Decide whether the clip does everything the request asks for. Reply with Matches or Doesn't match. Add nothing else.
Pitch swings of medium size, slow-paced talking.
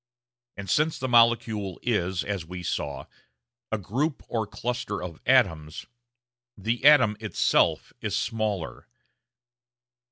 Matches